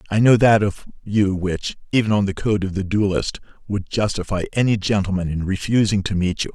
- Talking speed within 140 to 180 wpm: No, average, 200 wpm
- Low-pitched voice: Yes, low, 100 Hz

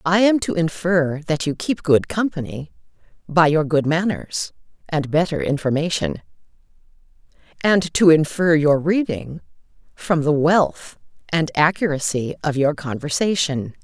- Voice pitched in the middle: Yes, medium, 155 Hz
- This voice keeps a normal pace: No, slow, 125 wpm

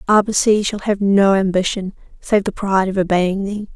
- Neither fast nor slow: Yes, average, 175 wpm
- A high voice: Yes, high, 195 Hz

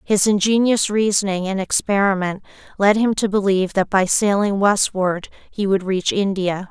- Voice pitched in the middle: No, high, 200 Hz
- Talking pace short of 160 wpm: Yes, average, 150 wpm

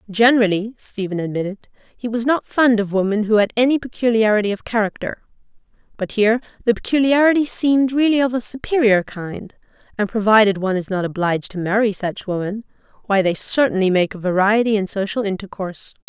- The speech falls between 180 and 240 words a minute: No, average, 165 wpm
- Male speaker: No, female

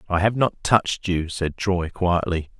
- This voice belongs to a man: Yes, male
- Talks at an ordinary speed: Yes, average, 185 wpm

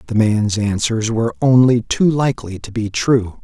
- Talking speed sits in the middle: Yes, average, 175 wpm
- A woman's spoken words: No, male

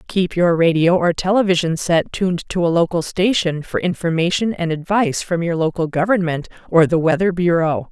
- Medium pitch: Yes, medium, 170 Hz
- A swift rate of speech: No, average, 175 wpm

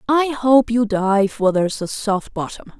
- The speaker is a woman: Yes, female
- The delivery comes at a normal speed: No, fast, 215 wpm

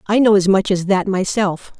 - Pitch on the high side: Yes, high, 195 Hz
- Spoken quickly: Yes, fast, 235 wpm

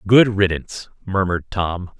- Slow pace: Yes, slow, 120 wpm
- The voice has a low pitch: Yes, very low, 95 Hz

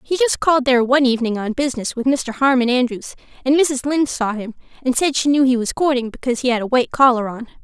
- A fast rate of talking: Yes, fast, 245 wpm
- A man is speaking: No, female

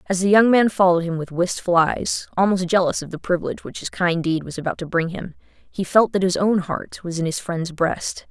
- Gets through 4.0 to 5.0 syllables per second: No, 5.4 syllables/s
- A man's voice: No, female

